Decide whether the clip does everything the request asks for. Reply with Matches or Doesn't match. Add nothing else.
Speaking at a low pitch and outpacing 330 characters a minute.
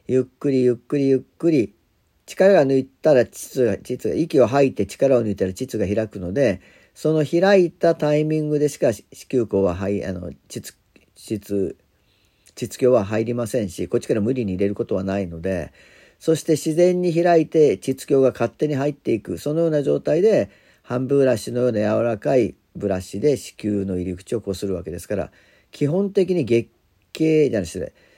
Matches